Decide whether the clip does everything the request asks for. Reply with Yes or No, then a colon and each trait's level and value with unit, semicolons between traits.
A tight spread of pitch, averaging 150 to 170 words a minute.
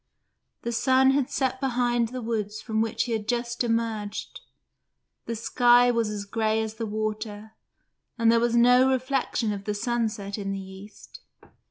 Yes: narrow, 2.3 semitones; average, 165 wpm